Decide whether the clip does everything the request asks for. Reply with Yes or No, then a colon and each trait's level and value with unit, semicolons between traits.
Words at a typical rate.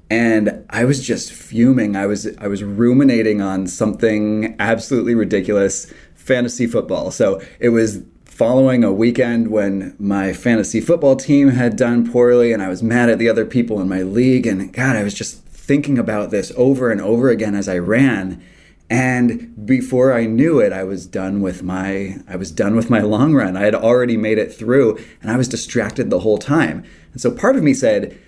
Yes: average, 195 wpm